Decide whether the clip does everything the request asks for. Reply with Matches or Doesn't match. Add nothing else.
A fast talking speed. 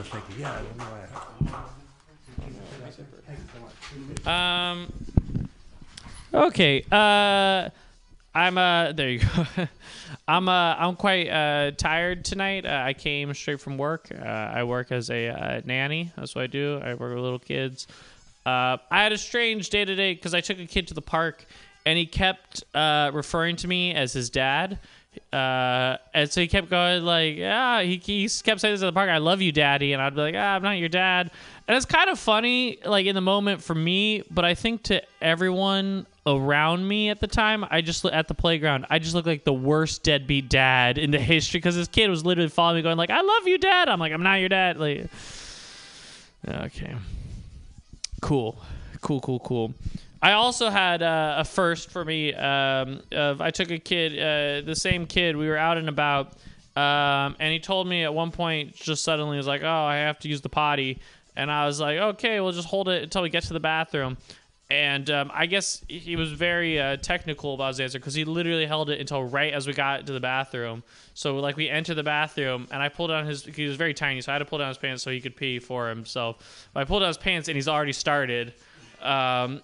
Matches